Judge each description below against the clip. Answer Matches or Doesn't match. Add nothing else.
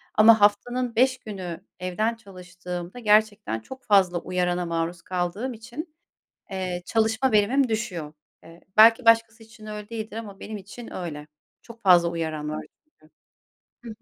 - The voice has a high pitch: Matches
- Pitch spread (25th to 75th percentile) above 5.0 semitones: Doesn't match